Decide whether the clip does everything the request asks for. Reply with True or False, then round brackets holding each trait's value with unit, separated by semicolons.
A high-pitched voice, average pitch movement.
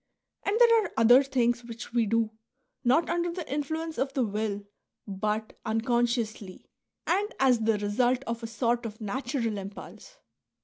True (240 Hz; 3.8 semitones)